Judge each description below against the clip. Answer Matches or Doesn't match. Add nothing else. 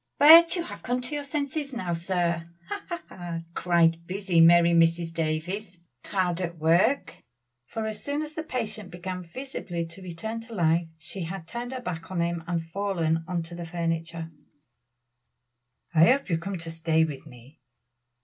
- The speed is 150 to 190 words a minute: Matches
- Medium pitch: Matches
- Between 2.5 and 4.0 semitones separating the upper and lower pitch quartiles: Doesn't match